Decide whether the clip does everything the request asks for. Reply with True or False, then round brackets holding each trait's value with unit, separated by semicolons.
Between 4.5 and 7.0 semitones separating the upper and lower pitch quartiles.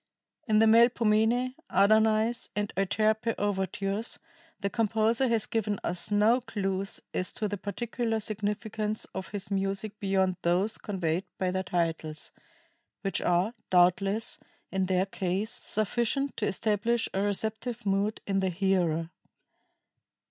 False (2.5 semitones)